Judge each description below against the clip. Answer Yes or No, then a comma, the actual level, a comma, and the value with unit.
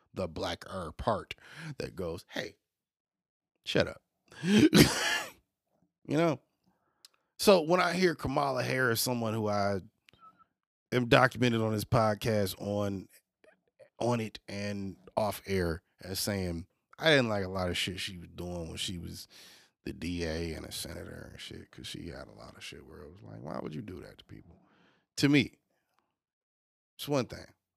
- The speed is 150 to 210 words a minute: Yes, average, 165 wpm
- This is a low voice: Yes, low, 100 Hz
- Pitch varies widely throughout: Yes, wide, 5.7 semitones